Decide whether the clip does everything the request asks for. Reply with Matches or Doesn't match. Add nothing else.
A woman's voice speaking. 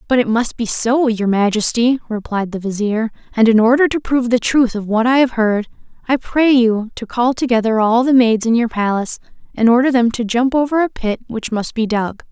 Matches